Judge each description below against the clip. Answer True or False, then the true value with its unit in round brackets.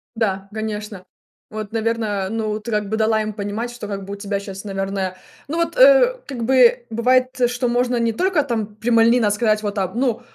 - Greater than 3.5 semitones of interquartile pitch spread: False (2.8 semitones)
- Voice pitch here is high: True (220 Hz)